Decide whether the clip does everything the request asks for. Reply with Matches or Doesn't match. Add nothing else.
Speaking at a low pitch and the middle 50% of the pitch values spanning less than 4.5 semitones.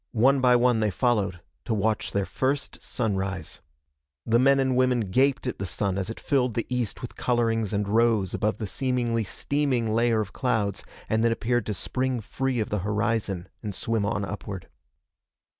Matches